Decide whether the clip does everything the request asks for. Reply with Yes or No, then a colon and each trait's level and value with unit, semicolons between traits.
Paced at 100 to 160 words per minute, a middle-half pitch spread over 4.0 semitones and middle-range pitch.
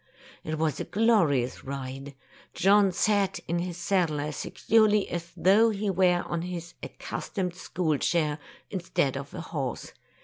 Yes: average, 145 wpm; average, 4.5 semitones; medium, 175 Hz